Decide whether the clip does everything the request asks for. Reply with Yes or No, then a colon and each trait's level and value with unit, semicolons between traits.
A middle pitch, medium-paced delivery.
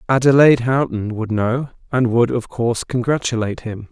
No: low, 120 Hz; average, 155 wpm